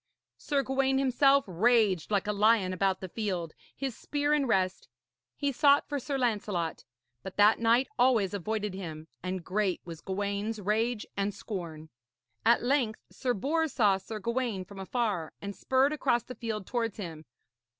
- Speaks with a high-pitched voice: Yes, high, 215 Hz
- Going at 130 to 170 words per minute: Yes, average, 160 wpm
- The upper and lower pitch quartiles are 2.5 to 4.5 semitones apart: No, average, 4.9 semitones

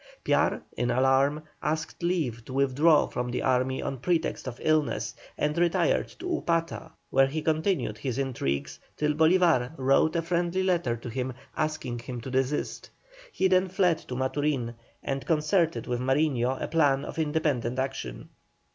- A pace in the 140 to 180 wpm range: Yes, average, 155 wpm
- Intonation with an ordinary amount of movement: Yes, average, 4.2 semitones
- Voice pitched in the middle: Yes, medium, 145 Hz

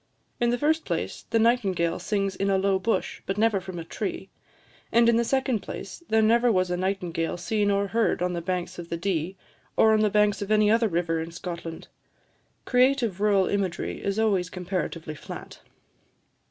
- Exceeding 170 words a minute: Yes, average, 190 wpm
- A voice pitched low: No, high, 200 Hz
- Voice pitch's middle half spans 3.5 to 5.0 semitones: Yes, average, 3.8 semitones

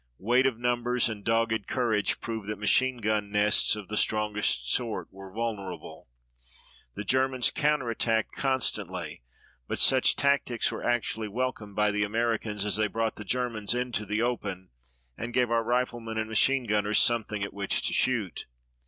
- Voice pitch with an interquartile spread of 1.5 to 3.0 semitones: Yes, average, 2.7 semitones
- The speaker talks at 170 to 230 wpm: No, average, 160 wpm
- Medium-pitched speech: No, low, 110 Hz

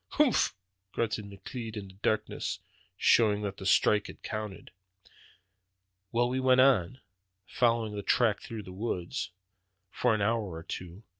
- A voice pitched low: Yes, low, 110 Hz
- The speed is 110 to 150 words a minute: Yes, average, 145 wpm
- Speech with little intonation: No, average, 3.0 semitones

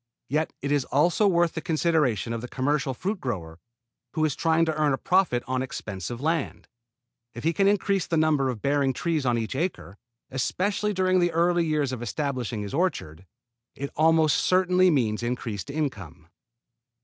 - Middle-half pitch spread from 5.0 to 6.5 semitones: Yes, wide, 5.6 semitones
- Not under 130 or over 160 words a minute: No, average, 175 wpm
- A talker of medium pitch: Yes, medium, 145 Hz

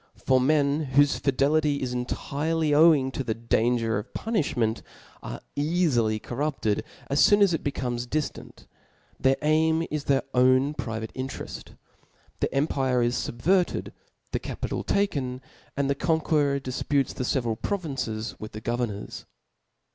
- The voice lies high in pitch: No, low, 135 Hz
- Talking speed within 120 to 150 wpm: Yes, average, 140 wpm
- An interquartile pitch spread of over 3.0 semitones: Yes, average, 3.9 semitones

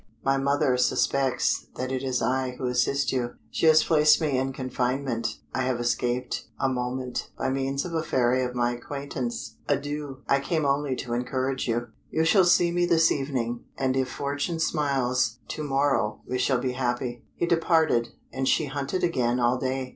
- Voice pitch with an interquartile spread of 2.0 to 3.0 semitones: Yes, narrow, 2.4 semitones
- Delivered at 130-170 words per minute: No, average, 180 wpm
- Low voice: Yes, low, 130 Hz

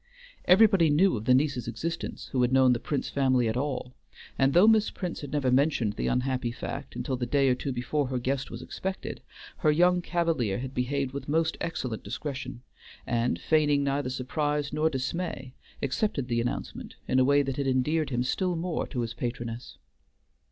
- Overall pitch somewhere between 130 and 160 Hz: Yes, low, 135 Hz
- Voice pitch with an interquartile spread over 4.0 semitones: No, average, 3.6 semitones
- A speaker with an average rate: Yes, average, 185 wpm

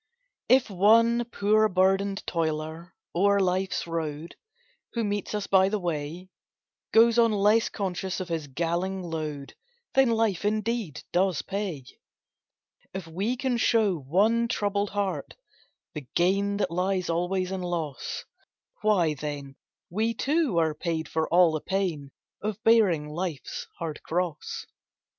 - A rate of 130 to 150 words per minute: Yes, slow, 135 wpm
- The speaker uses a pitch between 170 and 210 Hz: Yes, medium, 185 Hz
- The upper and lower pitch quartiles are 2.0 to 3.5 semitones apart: No, average, 4.2 semitones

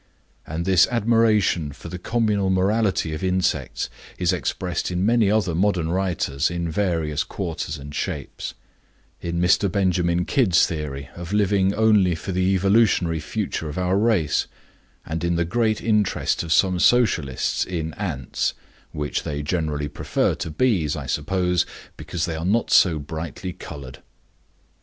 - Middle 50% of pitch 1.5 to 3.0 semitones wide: No, average, 3.9 semitones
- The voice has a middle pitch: No, very low, 90 Hz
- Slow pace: No, average, 145 wpm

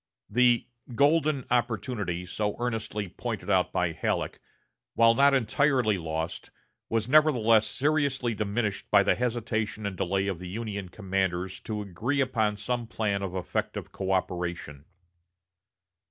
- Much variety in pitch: No, average, 4.2 semitones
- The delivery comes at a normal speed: No, slow, 125 wpm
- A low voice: Yes, low, 110 Hz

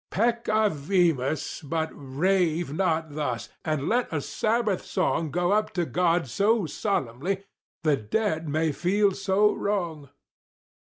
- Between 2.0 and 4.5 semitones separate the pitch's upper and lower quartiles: No, average, 4.9 semitones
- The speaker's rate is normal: No, slow, 120 wpm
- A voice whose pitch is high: No, medium, 170 Hz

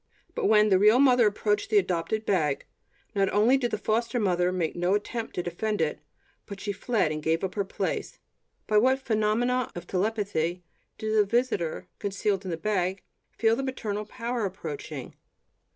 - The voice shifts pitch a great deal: No, average, 3.8 semitones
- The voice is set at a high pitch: Yes, high, 210 Hz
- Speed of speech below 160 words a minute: No, average, 175 wpm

